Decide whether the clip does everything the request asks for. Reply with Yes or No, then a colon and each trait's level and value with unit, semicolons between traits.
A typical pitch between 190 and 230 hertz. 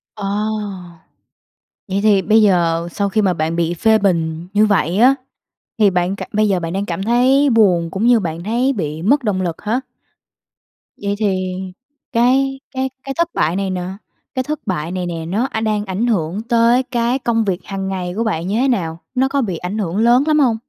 Yes: high, 205 Hz